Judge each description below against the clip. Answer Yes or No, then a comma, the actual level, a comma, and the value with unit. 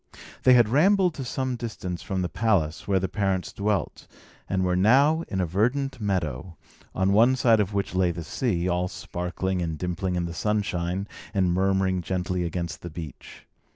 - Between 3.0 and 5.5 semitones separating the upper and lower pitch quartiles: Yes, average, 3.7 semitones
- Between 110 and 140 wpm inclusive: No, average, 180 wpm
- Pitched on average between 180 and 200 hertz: No, very low, 95 Hz